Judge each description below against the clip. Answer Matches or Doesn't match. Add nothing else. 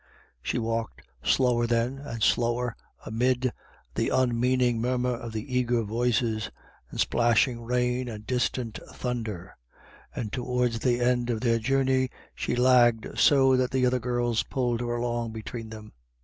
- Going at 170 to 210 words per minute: Doesn't match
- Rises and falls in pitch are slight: Matches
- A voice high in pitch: Doesn't match